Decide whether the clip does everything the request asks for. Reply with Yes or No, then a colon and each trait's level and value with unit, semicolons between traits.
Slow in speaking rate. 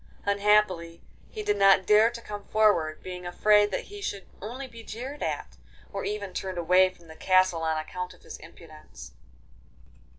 No: average, 170 wpm